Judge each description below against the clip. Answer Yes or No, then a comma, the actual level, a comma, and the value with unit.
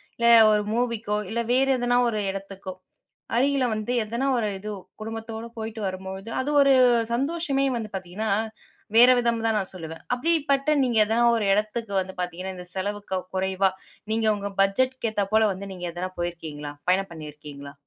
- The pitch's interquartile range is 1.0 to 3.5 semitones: No, average, 3.9 semitones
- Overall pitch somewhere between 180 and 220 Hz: Yes, high, 215 Hz